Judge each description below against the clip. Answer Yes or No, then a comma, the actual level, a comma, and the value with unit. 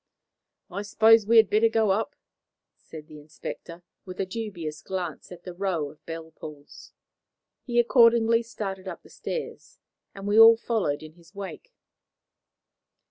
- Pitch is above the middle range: Yes, high, 195 Hz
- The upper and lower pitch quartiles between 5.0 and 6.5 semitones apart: Yes, wide, 5.4 semitones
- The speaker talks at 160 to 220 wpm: No, average, 150 wpm